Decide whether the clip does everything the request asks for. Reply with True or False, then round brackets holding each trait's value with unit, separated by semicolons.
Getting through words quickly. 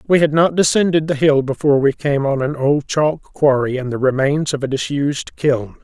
True (215 wpm)